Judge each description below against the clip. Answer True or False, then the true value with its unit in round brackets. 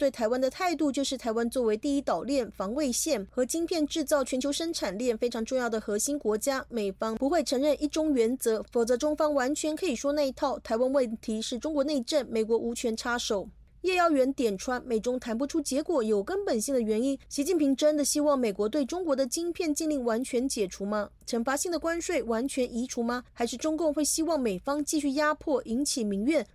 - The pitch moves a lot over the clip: False (4.2 semitones)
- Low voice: False (265 Hz)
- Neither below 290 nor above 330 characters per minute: True (325 characters per minute)